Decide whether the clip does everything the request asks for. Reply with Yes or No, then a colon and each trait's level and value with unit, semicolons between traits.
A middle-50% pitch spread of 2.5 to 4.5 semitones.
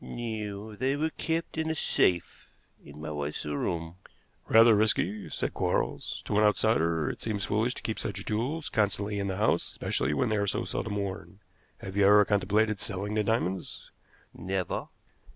Yes: average, 2.8 semitones